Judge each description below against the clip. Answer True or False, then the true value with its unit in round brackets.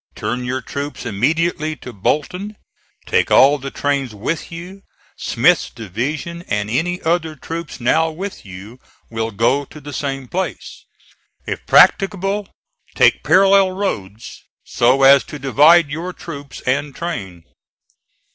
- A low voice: False (145 Hz)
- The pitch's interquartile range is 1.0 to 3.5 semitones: False (5.4 semitones)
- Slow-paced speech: True (130 wpm)